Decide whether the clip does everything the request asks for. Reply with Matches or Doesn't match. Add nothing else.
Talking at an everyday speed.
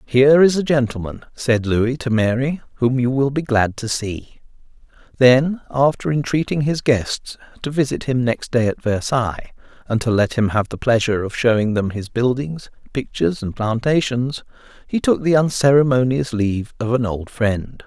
Matches